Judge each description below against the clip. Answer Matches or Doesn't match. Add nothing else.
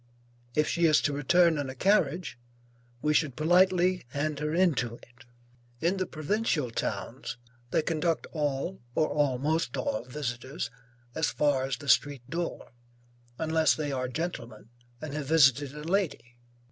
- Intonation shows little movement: Doesn't match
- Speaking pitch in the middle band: Matches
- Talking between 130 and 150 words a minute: Matches